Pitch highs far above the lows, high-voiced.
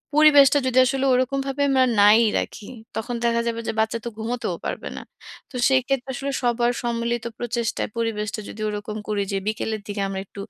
No: average, 3.1 semitones; high, 235 Hz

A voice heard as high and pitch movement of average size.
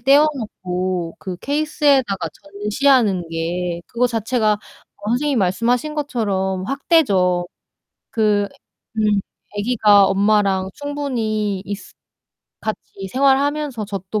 No: high, 210 Hz; wide, 5.7 semitones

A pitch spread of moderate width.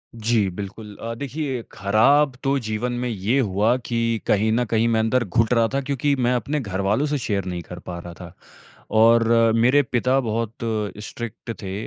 Yes: average, 3.4 semitones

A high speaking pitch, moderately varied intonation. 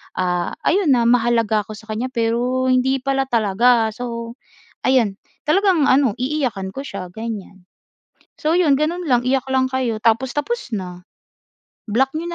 Yes: high, 245 Hz; average, 3.5 semitones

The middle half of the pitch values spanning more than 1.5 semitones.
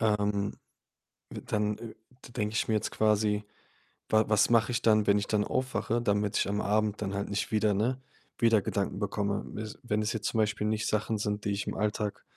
No: narrow, 1.1 semitones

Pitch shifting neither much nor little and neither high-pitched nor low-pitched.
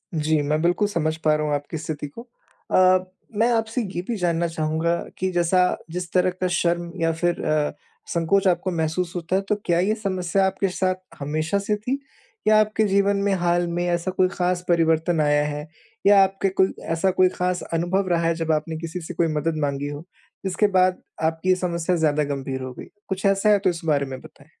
Yes: average, 3.0 semitones; medium, 175 Hz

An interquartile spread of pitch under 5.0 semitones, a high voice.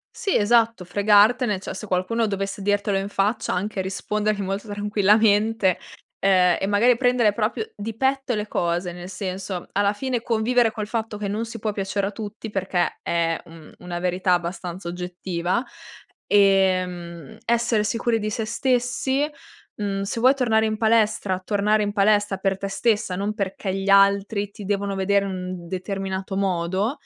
Yes: narrow, 2.6 semitones; high, 200 Hz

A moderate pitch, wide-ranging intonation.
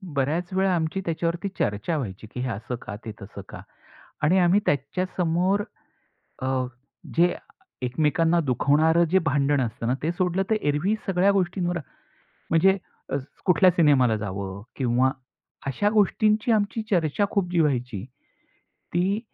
Yes: medium, 165 Hz; wide, 6.1 semitones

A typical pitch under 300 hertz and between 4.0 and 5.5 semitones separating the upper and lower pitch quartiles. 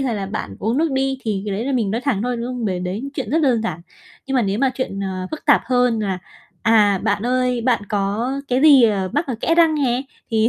Yes: high, 235 Hz; average, 4.6 semitones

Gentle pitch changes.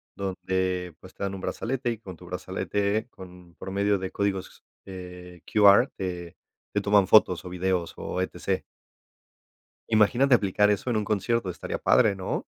Yes: narrow, 2.2 semitones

